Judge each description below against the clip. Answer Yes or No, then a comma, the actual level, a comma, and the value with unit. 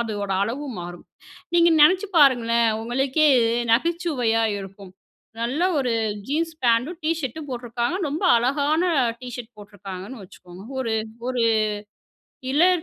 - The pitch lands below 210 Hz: No, very high, 250 Hz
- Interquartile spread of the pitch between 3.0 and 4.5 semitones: No, average, 5.0 semitones